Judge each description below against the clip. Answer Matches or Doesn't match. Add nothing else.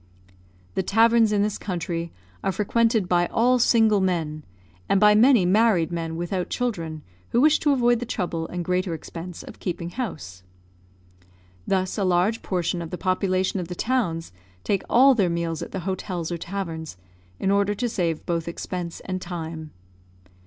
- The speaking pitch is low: Doesn't match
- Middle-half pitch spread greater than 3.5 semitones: Matches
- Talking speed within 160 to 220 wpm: Matches